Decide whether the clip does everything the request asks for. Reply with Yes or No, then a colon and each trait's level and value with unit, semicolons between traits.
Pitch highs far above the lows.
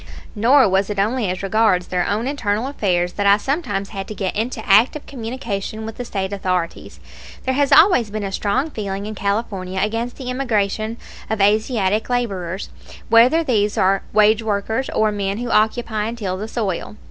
No: average, 3.1 semitones